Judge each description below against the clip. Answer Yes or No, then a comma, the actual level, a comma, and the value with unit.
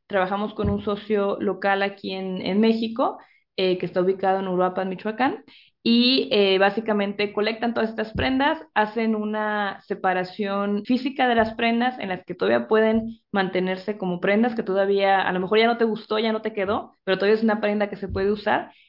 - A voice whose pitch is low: No, high, 205 Hz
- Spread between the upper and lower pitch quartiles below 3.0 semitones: Yes, narrow, 2.4 semitones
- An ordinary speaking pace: No, fast, 195 wpm